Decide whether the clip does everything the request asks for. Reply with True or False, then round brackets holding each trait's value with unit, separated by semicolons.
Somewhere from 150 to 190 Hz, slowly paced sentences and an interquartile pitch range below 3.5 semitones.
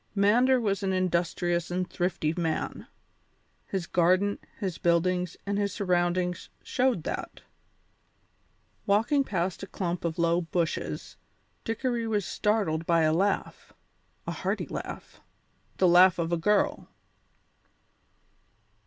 True (185 Hz; 120 wpm; 2.9 semitones)